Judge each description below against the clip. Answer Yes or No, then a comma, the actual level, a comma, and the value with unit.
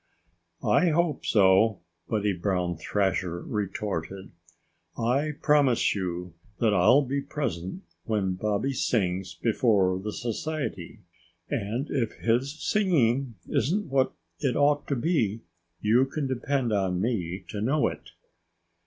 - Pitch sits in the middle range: No, low, 115 Hz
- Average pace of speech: No, slow, 120 wpm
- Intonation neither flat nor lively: No, wide, 6.3 semitones